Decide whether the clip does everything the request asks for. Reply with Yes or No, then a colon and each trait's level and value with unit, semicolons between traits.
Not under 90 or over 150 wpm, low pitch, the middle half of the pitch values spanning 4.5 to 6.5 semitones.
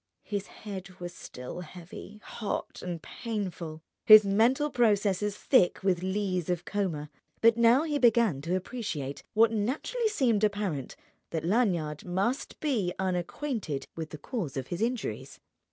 No: average, 140 wpm; high, 200 Hz; average, 4.8 semitones